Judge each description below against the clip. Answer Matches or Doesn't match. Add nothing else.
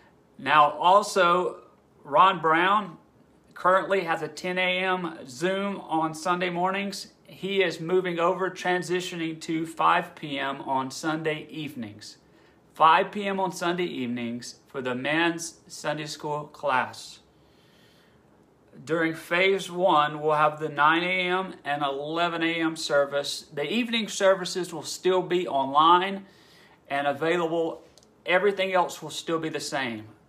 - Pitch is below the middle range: Doesn't match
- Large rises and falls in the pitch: Doesn't match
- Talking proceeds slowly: Matches